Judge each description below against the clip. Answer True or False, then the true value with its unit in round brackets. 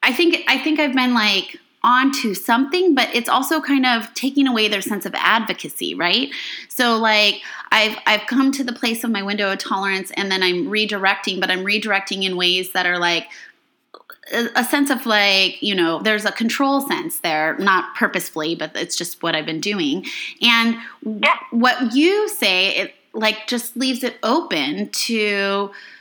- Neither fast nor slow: True (180 wpm)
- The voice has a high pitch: True (230 Hz)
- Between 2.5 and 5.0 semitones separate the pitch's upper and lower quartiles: False (5.4 semitones)